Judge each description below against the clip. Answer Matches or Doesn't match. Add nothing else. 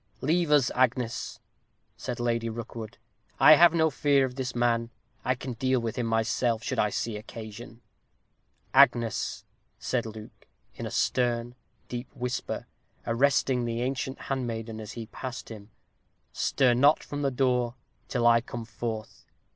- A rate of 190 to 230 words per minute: Doesn't match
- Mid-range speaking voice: Doesn't match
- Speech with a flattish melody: Matches